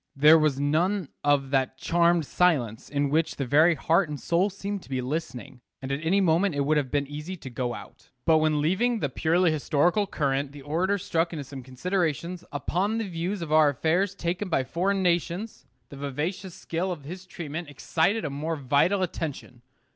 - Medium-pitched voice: Yes, medium, 160 Hz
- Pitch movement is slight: No, average, 4.0 semitones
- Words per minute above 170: Yes, average, 190 wpm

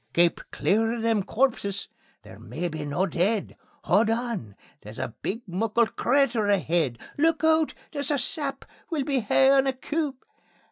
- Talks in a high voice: Yes, high, 225 Hz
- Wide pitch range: Yes, wide, 6.3 semitones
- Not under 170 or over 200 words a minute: No, average, 150 wpm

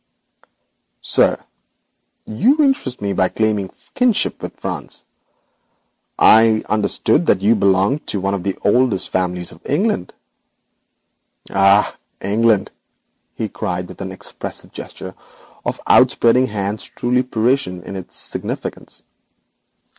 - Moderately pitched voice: No, low, 105 Hz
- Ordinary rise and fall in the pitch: Yes, average, 4.2 semitones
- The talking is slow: Yes, slow, 115 wpm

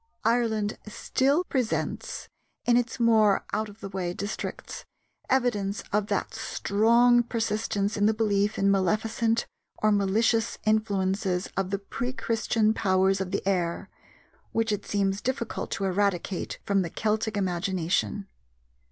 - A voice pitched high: Yes, high, 210 Hz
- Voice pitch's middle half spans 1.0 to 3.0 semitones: Yes, narrow, 2.5 semitones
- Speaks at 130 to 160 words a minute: Yes, slow, 135 wpm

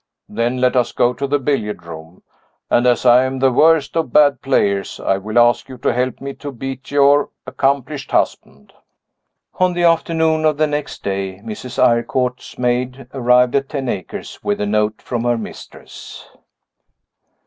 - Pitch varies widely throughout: No, average, 3.1 semitones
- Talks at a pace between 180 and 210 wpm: No, average, 170 wpm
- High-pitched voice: No, low, 125 Hz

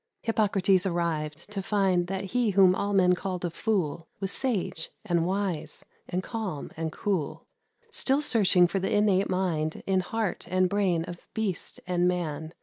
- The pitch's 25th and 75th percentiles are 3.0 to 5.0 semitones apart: No, narrow, 2.6 semitones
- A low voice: No, medium, 185 Hz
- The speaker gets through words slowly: No, average, 160 wpm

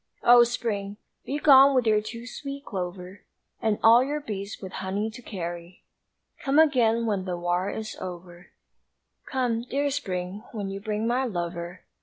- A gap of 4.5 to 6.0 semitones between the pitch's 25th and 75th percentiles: Yes, average, 4.8 semitones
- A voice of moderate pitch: No, high, 215 Hz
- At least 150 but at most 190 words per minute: Yes, average, 155 wpm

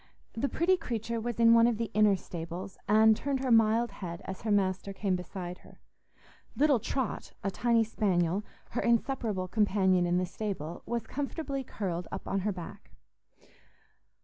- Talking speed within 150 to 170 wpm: Yes, average, 165 wpm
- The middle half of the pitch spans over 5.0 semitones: No, average, 3.8 semitones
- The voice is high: Yes, high, 210 Hz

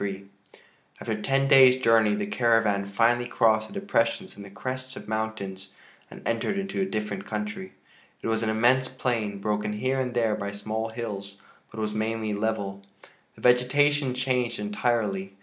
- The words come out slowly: No, average, 165 wpm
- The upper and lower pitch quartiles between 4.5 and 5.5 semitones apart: No, average, 3.2 semitones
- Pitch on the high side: No, low, 110 Hz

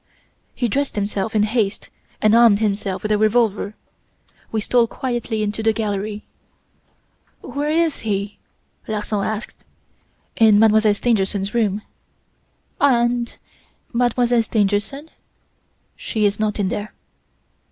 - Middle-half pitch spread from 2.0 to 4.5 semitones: Yes, narrow, 2.5 semitones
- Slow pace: Yes, slow, 115 wpm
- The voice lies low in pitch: No, high, 215 Hz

